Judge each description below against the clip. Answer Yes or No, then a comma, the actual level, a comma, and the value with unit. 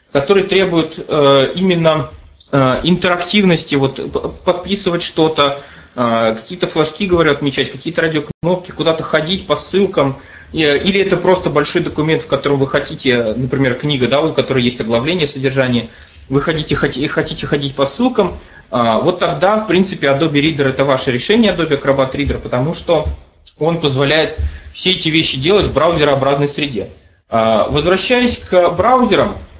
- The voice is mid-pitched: Yes, medium, 150 Hz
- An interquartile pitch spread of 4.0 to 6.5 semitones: Yes, average, 4.5 semitones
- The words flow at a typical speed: Yes, average, 135 wpm